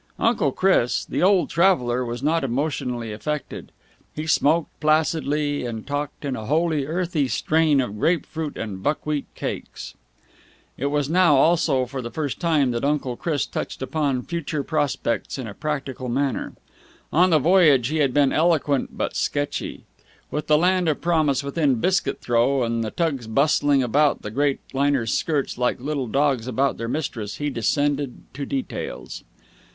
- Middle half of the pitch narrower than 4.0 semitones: Yes, average, 3.4 semitones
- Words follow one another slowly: No, average, 160 wpm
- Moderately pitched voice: Yes, medium, 145 Hz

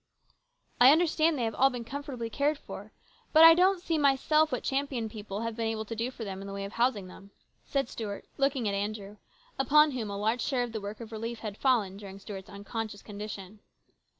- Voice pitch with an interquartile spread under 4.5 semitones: No, average, 5.0 semitones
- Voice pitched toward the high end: Yes, high, 230 Hz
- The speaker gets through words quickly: Yes, fast, 220 wpm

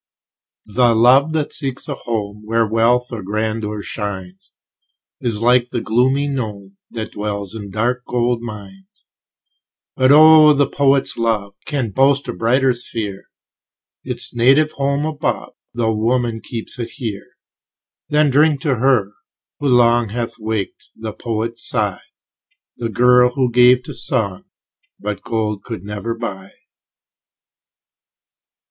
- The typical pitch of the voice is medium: No, low, 115 Hz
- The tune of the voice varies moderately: Yes, average, 3.3 semitones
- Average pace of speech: No, slow, 130 wpm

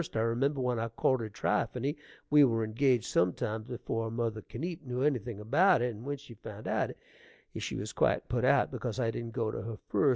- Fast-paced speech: Yes, fast, 215 wpm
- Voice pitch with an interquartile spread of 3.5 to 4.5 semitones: No, average, 3.0 semitones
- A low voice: Yes, low, 120 Hz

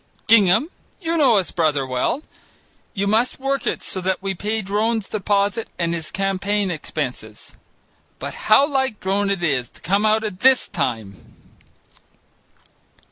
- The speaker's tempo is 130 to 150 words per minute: Yes, average, 145 wpm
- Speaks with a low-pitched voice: No, high, 200 Hz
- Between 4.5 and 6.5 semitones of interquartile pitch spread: No, average, 3.8 semitones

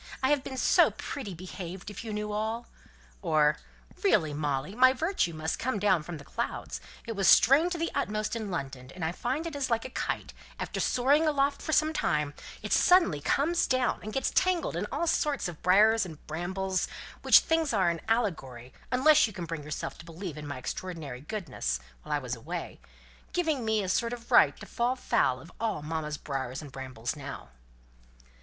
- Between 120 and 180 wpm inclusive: No, average, 195 wpm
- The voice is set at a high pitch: Yes, high, 195 Hz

